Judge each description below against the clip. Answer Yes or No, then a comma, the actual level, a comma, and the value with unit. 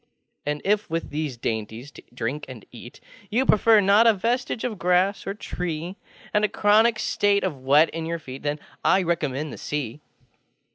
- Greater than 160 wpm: Yes, average, 175 wpm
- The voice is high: No, medium, 165 Hz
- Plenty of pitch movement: Yes, wide, 6.1 semitones